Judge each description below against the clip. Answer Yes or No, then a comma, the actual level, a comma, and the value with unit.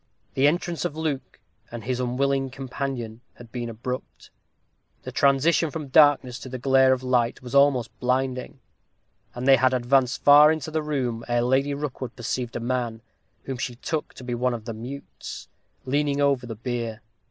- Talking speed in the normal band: Yes, average, 175 wpm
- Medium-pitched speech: No, low, 130 Hz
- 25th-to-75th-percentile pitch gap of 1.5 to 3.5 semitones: Yes, narrow, 2.4 semitones